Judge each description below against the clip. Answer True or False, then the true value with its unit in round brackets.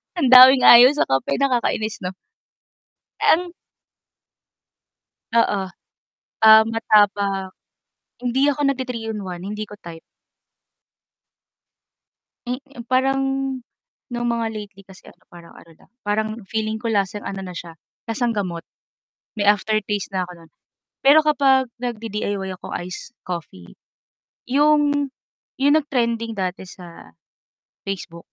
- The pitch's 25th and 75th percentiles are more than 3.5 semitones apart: True (4.6 semitones)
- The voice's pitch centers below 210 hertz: False (215 Hz)